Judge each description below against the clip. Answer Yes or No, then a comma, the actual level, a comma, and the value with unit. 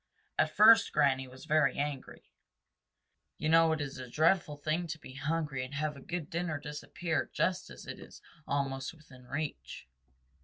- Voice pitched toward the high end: No, medium, 150 Hz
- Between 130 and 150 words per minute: No, average, 165 wpm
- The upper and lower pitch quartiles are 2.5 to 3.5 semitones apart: Yes, average, 2.8 semitones